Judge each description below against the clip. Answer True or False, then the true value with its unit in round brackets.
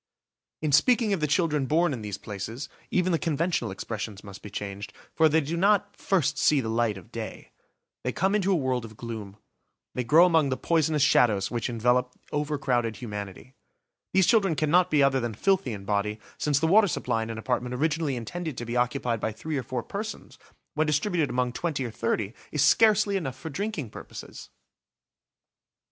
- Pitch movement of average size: False (6.3 semitones)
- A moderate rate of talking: True (190 wpm)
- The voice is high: False (135 Hz)